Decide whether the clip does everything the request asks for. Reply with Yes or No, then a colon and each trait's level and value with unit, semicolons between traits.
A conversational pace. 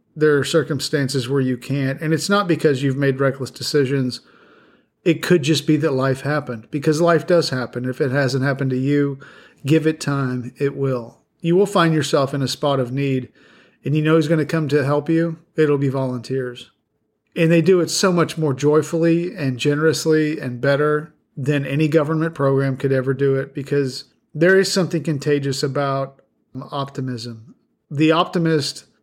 Yes: average, 180 wpm